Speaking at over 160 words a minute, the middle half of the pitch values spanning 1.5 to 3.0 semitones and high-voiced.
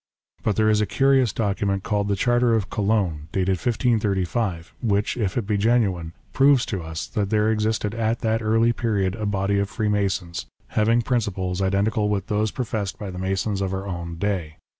No: average, 185 wpm; narrow, 2.6 semitones; low, 105 Hz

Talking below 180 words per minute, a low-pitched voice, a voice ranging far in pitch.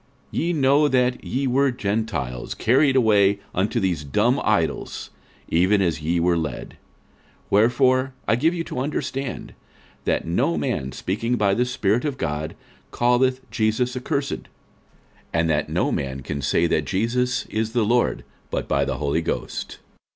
Yes: average, 160 wpm; low, 115 Hz; wide, 6.7 semitones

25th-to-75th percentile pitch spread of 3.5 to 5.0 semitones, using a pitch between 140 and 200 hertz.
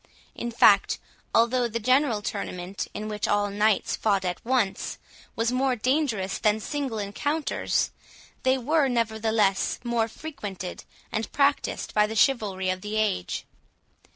No: average, 3.8 semitones; high, 220 Hz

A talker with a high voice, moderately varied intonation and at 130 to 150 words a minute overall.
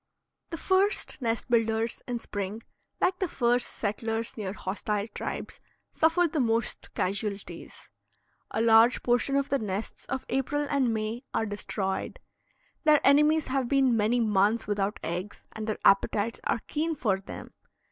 Yes: high, 230 Hz; average, 4.6 semitones; average, 145 wpm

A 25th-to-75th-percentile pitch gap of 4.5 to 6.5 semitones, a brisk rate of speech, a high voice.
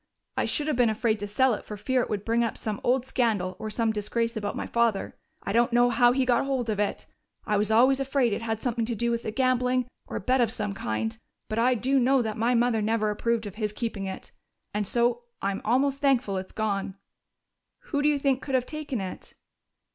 No: average, 3.3 semitones; fast, 230 wpm; high, 235 Hz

